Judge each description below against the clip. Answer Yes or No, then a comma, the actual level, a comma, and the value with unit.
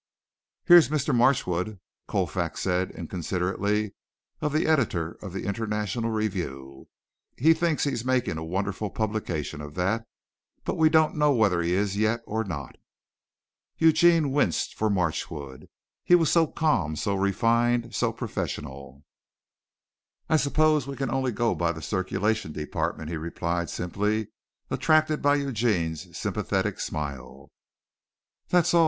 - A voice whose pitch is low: Yes, low, 105 Hz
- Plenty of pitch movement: Yes, wide, 8.2 semitones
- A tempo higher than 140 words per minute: No, slow, 135 wpm